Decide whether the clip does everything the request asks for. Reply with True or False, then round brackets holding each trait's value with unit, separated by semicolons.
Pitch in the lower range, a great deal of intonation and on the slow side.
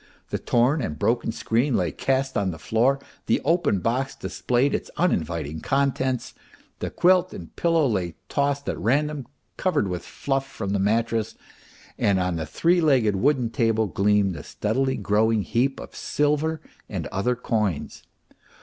False (115 Hz; 5.7 semitones; 155 wpm)